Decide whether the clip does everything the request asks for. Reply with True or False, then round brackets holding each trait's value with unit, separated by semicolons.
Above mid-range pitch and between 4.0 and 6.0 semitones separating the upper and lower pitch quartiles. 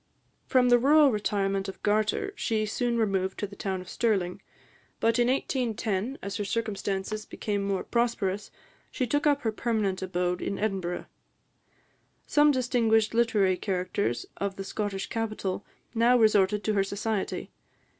False (210 Hz; 3.3 semitones)